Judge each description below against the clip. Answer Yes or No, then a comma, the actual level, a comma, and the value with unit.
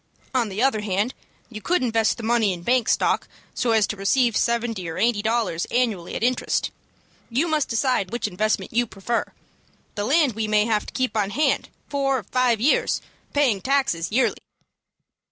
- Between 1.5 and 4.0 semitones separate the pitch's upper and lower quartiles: Yes, average, 3.3 semitones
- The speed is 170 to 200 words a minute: Yes, average, 180 wpm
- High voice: Yes, high, 230 Hz